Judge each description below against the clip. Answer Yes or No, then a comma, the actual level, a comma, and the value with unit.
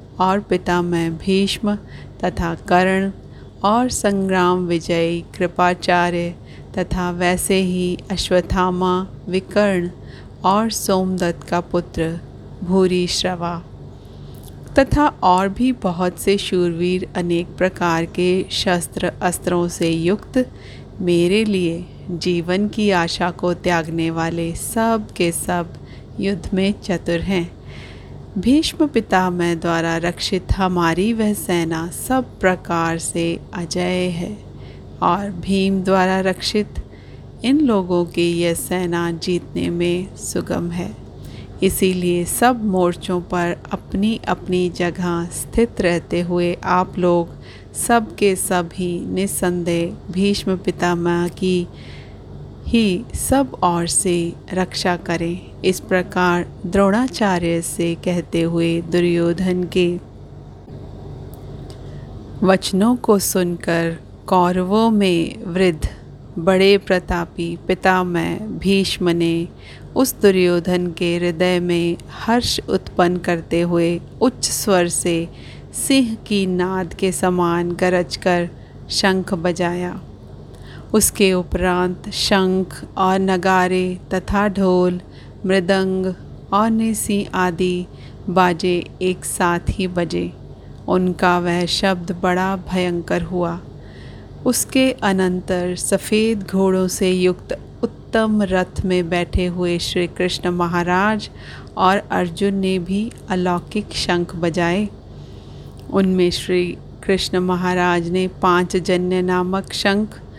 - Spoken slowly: Yes, slow, 105 wpm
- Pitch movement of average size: No, narrow, 1.7 semitones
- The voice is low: No, medium, 180 Hz